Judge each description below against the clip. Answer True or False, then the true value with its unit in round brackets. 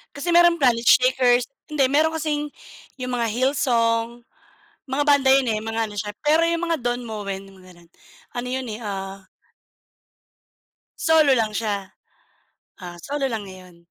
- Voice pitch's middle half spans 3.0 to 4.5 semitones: False (5.5 semitones)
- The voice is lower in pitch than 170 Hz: False (240 Hz)